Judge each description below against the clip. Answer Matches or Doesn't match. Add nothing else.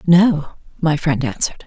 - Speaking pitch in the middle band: Matches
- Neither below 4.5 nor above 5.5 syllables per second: Matches